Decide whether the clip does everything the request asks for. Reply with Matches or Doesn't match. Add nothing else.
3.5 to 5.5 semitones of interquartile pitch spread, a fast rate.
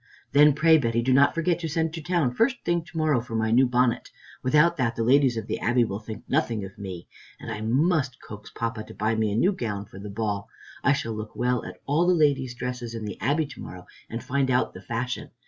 Matches